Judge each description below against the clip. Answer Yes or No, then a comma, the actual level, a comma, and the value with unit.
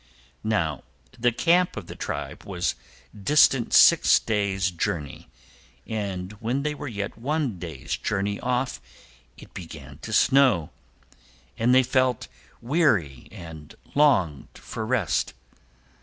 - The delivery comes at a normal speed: No, slow, 120 wpm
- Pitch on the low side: Yes, low, 110 Hz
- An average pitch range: No, wide, 6.6 semitones